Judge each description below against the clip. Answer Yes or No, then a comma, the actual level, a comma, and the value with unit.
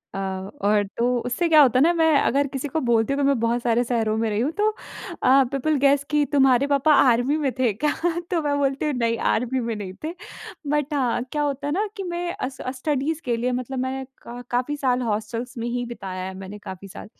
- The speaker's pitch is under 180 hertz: No, very high, 255 Hz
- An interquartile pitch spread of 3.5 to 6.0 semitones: Yes, average, 3.8 semitones